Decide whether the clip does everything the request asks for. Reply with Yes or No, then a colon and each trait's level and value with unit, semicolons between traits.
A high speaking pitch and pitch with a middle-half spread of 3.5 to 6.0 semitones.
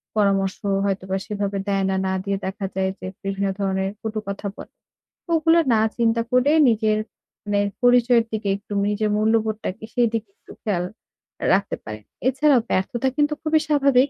Yes: high, 215 Hz; average, 3.8 semitones